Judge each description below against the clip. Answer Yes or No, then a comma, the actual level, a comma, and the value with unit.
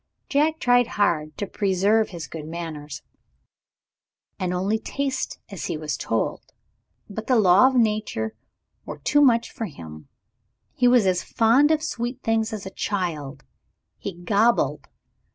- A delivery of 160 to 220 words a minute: No, average, 145 wpm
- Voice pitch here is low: No, high, 205 Hz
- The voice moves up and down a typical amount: No, wide, 6.1 semitones